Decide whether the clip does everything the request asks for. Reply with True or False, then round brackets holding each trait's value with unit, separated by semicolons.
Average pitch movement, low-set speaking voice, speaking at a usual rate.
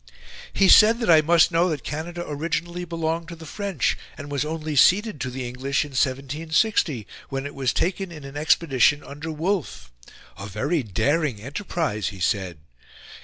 False (4.2 semitones; 150 Hz; 170 wpm)